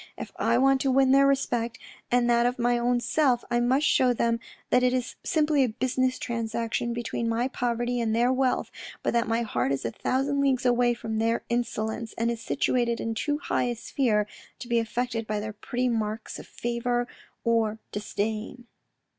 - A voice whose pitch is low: No, high, 240 Hz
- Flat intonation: Yes, narrow, 1.8 semitones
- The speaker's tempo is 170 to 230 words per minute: Yes, average, 190 wpm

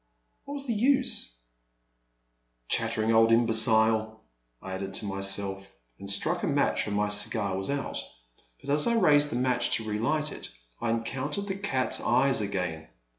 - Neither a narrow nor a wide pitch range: No, wide, 6.2 semitones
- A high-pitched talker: No, low, 110 Hz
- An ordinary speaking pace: Yes, average, 175 wpm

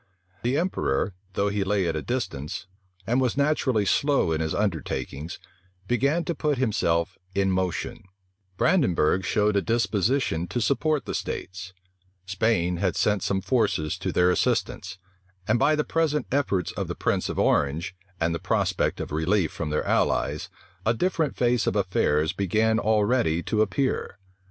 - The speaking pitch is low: Yes, low, 100 Hz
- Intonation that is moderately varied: No, wide, 6.2 semitones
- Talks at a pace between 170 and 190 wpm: No, average, 155 wpm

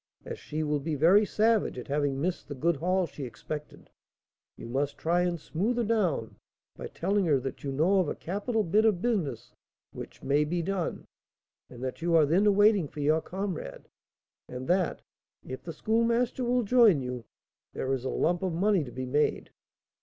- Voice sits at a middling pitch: Yes, medium, 170 Hz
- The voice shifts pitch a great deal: Yes, wide, 5.9 semitones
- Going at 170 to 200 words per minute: Yes, average, 190 wpm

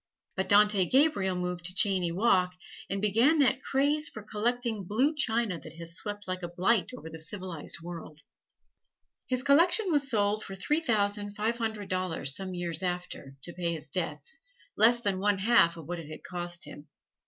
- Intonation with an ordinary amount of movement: Yes, average, 4.9 semitones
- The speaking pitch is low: No, high, 195 Hz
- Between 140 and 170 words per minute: No, average, 180 wpm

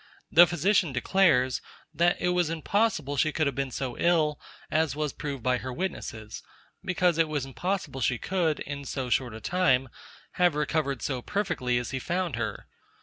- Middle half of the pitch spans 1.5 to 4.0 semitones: No, average, 5.1 semitones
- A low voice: No, medium, 150 Hz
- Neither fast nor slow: Yes, average, 170 wpm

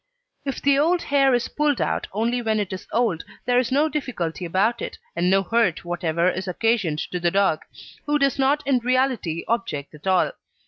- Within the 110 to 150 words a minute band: No, average, 195 wpm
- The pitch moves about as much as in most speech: No, wide, 6.8 semitones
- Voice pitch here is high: Yes, high, 230 Hz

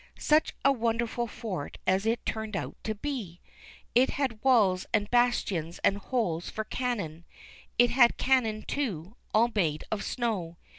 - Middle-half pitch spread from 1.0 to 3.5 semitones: No, average, 4.3 semitones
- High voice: Yes, high, 220 Hz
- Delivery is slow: No, average, 150 wpm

